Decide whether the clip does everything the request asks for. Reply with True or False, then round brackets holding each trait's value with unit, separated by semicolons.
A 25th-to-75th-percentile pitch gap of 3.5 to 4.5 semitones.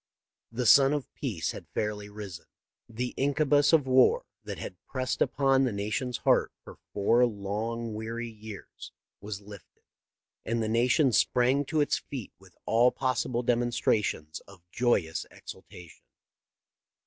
True (3.9 semitones)